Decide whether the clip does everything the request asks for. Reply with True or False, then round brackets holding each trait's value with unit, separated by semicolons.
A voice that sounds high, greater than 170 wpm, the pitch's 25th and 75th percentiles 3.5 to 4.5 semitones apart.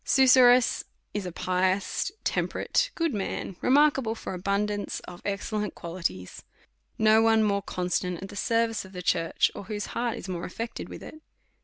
False (205 Hz; 165 wpm; 3.9 semitones)